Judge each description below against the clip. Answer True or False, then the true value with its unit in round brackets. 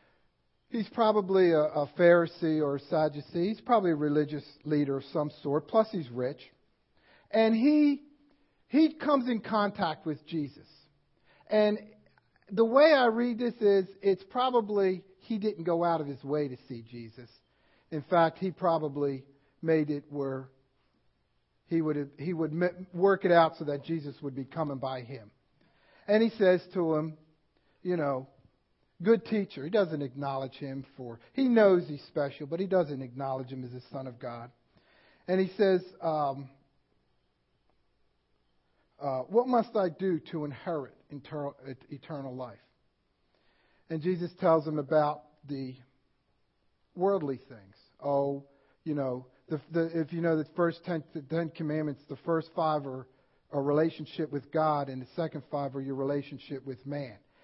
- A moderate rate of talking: True (155 wpm)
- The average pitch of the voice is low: False (155 Hz)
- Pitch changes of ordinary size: True (4.8 semitones)